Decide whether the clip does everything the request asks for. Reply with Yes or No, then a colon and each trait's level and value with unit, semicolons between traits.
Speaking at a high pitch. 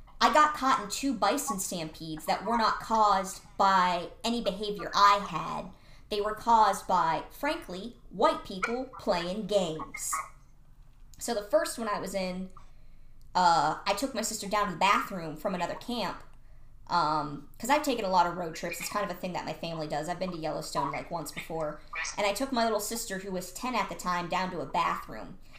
Yes: high, 195 Hz